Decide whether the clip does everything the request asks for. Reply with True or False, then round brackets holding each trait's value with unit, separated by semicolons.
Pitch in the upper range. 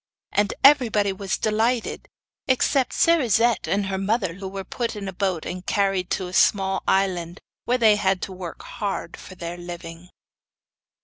True (195 Hz)